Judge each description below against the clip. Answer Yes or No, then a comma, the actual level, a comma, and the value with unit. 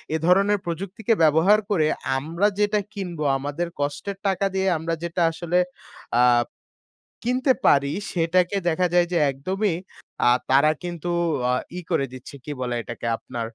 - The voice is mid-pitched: Yes, medium, 175 Hz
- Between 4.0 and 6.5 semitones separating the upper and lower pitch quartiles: Yes, average, 4.7 semitones